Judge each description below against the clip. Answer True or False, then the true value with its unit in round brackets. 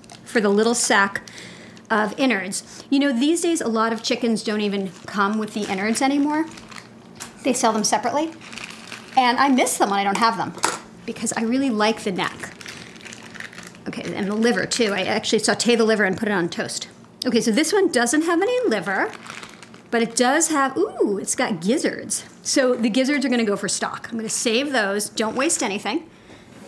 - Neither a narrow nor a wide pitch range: True (3.9 semitones)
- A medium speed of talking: True (195 wpm)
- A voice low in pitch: False (230 Hz)